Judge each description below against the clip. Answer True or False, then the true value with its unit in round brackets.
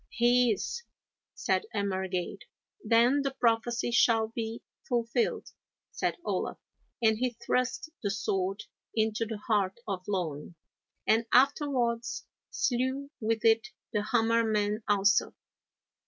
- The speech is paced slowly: True (115 wpm)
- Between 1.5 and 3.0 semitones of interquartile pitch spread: True (2.7 semitones)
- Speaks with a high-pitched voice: True (225 Hz)